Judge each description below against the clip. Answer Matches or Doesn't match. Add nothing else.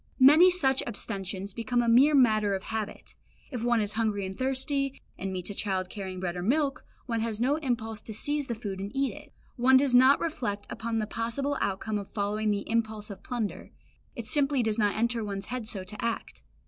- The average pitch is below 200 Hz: Doesn't match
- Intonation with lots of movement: Doesn't match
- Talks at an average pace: Doesn't match